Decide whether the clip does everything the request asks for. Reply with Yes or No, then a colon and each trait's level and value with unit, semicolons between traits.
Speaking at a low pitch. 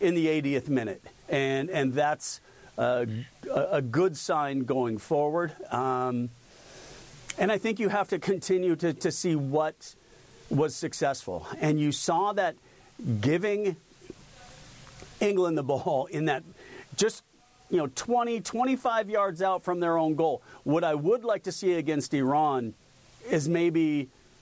No: medium, 160 Hz